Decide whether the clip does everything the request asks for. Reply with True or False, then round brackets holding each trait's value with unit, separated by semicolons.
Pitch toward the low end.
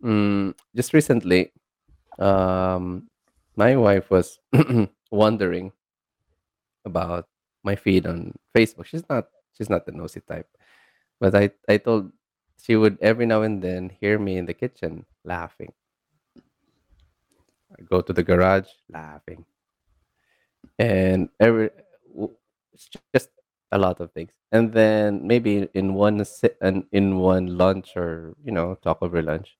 True (95 Hz)